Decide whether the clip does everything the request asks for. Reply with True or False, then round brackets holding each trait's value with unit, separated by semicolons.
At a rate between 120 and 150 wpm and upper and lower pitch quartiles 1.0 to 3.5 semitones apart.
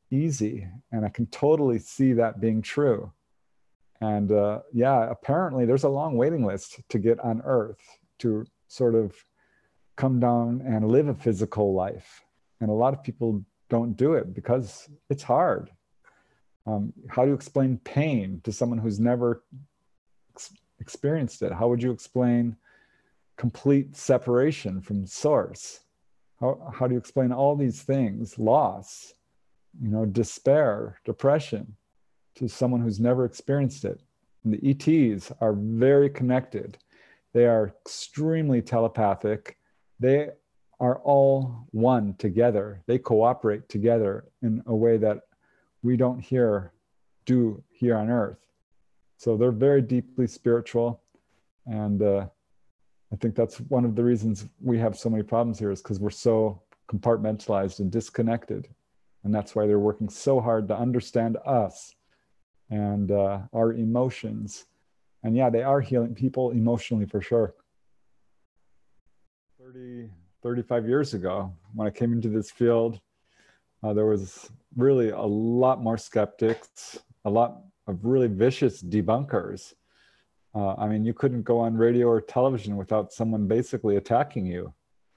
True (140 wpm; 2.9 semitones)